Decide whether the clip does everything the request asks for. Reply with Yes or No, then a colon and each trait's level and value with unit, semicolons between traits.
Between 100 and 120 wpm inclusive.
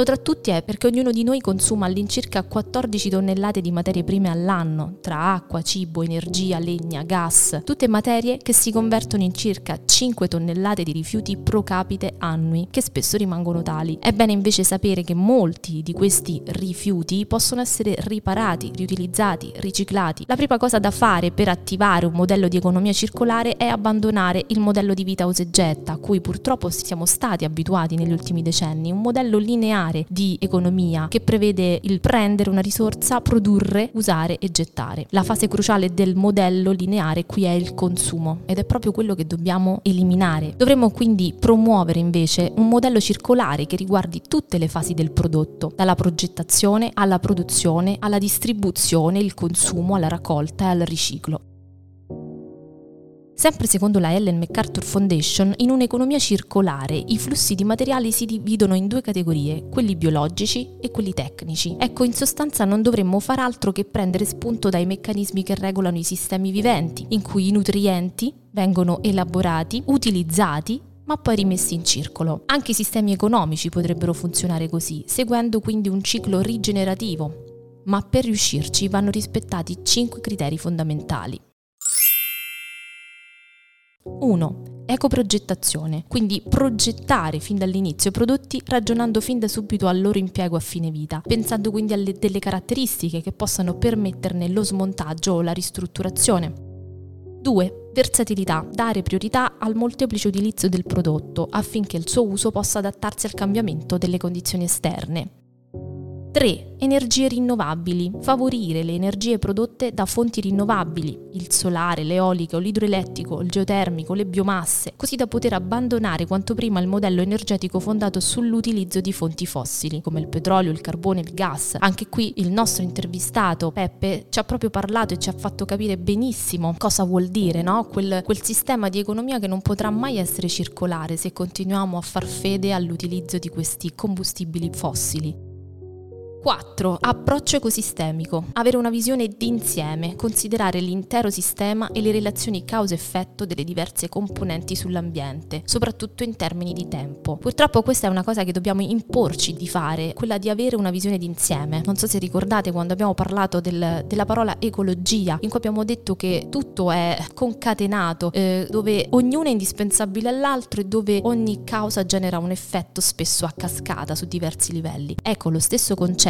No: average, 155 wpm